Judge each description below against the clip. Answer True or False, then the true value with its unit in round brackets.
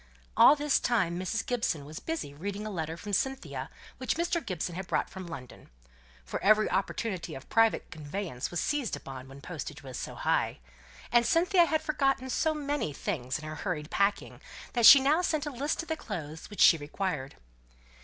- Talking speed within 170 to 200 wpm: True (185 wpm)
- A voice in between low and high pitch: False (200 Hz)